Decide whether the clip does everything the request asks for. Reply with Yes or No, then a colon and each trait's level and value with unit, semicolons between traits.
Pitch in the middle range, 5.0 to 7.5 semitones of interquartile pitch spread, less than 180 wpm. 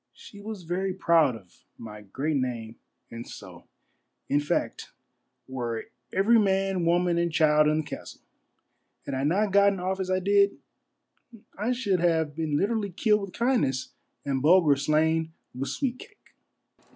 Yes: medium, 170 Hz; wide, 5.5 semitones; average, 150 wpm